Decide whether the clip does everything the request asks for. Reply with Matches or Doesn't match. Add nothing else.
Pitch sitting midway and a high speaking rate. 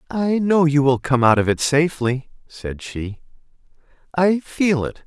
Doesn't match